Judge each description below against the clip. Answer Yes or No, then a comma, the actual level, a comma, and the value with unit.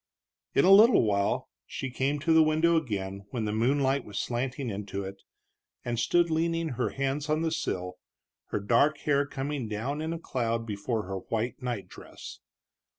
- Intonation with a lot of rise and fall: Yes, wide, 6.4 semitones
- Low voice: Yes, low, 130 Hz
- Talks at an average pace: Yes, average, 175 wpm